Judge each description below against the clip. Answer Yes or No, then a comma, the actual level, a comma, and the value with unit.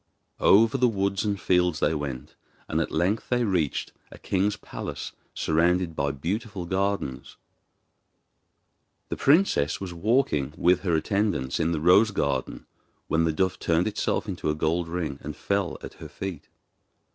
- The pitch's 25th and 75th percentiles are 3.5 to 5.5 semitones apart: Yes, average, 4.1 semitones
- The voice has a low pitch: Yes, very low, 90 Hz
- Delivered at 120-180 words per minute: Yes, average, 155 wpm